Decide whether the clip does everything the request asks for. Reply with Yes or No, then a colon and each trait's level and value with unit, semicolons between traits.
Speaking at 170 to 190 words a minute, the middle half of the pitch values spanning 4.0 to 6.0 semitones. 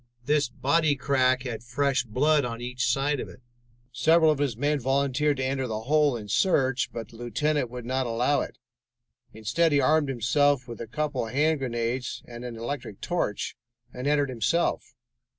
No: average, 175 wpm; average, 3.3 semitones